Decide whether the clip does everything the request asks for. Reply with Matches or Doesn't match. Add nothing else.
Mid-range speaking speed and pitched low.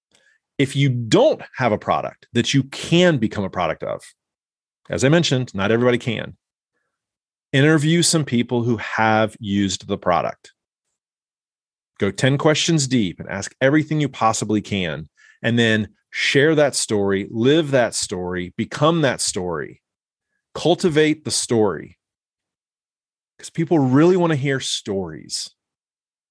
Doesn't match